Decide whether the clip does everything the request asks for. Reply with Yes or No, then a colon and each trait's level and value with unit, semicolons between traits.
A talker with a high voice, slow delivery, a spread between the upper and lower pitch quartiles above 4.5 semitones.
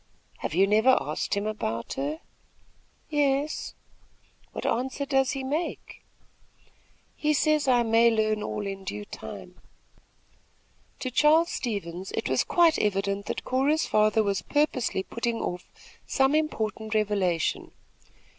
Yes: high, 225 Hz; slow, 125 wpm; wide, 5.5 semitones